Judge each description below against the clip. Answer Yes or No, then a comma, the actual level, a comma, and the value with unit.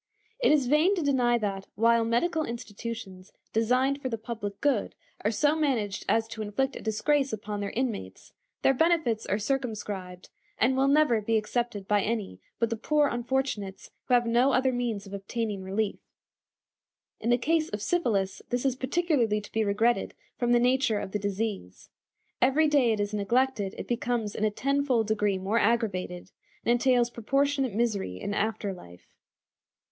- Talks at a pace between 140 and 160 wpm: No, average, 170 wpm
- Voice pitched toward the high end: Yes, high, 230 Hz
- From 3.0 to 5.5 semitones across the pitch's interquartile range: Yes, average, 4.2 semitones